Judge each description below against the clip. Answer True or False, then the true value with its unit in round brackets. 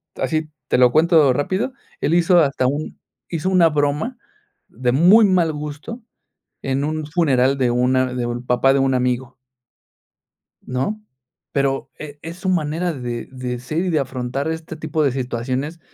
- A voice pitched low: False (145 Hz)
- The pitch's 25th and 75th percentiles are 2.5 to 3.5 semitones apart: False (4.3 semitones)